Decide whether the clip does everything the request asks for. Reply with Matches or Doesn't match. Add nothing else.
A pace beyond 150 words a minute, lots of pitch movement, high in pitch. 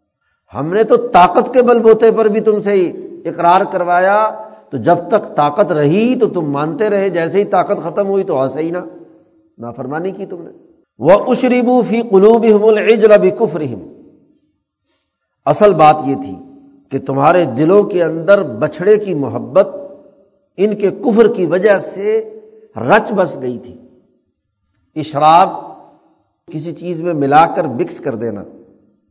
Doesn't match